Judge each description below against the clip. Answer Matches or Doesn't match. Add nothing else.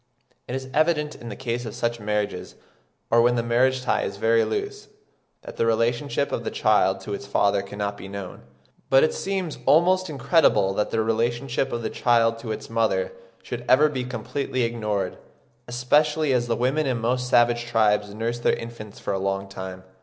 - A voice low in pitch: Matches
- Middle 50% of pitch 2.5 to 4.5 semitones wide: Matches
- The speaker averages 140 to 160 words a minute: Doesn't match